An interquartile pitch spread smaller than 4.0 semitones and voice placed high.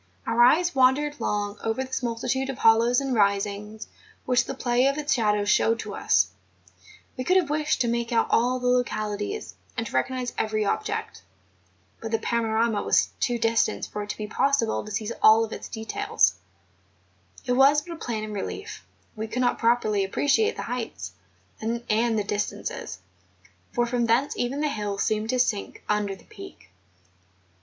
Yes: average, 3.2 semitones; high, 230 Hz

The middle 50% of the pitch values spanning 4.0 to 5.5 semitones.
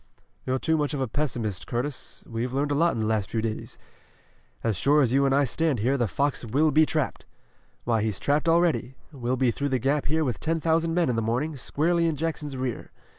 Yes: average, 4.3 semitones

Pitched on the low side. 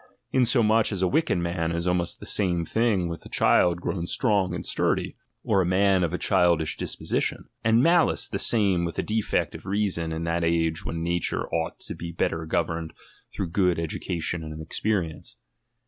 Yes: very low, 85 Hz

